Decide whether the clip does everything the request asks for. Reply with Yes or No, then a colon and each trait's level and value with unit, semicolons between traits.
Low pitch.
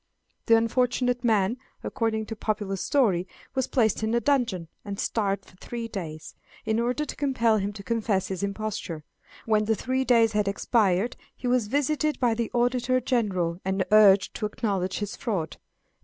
No: high, 220 Hz